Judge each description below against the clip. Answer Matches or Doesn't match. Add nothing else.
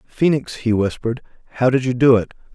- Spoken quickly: Doesn't match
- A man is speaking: Matches